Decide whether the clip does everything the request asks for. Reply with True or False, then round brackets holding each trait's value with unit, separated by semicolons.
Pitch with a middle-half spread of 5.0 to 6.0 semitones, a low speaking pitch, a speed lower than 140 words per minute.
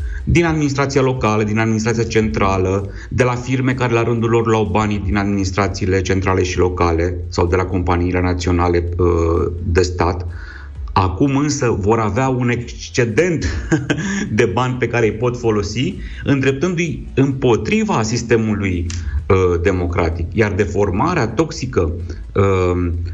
True (5.5 semitones; 105 Hz; 120 wpm)